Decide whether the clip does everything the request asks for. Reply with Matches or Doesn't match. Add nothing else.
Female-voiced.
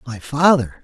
Doesn't match